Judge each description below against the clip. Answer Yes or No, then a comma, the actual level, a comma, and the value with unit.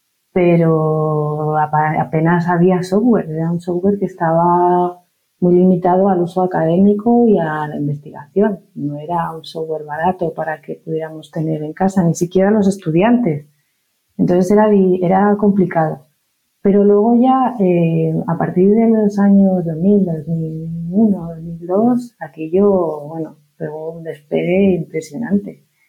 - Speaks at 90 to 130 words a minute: Yes, slow, 125 wpm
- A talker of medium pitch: Yes, medium, 175 Hz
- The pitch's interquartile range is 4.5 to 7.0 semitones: No, average, 3.6 semitones